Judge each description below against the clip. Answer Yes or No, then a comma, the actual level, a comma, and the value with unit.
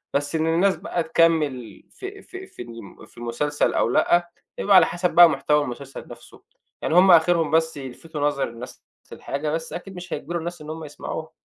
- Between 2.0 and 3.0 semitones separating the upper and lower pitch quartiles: No, average, 3.7 semitones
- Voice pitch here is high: No, medium, 160 Hz